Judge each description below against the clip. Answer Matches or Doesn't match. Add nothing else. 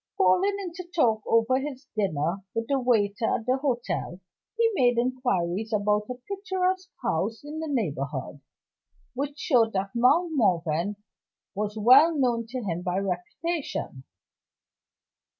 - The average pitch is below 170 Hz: Doesn't match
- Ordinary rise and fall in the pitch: Doesn't match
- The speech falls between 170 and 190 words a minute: Doesn't match